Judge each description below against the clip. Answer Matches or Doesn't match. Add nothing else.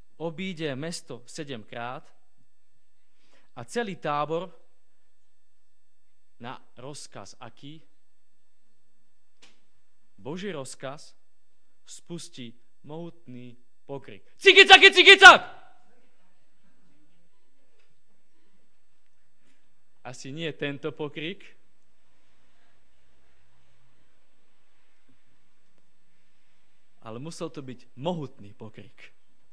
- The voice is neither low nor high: Doesn't match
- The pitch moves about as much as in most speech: Doesn't match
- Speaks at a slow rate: Matches